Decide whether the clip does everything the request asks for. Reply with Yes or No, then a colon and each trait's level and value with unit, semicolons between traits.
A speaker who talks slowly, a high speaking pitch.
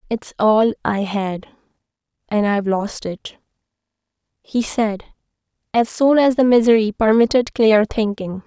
Yes: slow, 130 wpm; high, 220 Hz